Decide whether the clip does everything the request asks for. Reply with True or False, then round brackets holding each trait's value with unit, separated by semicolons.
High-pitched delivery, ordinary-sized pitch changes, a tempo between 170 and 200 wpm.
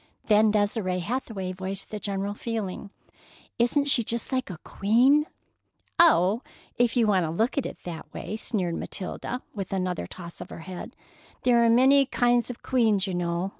True (210 Hz; 4.5 semitones; 180 wpm)